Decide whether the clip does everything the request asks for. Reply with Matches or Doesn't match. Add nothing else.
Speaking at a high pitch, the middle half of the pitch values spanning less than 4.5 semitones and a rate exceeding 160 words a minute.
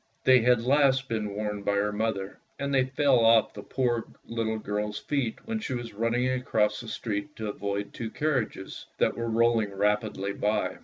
Doesn't match